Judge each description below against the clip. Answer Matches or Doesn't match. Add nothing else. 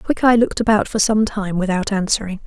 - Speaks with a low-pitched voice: Doesn't match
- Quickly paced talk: Doesn't match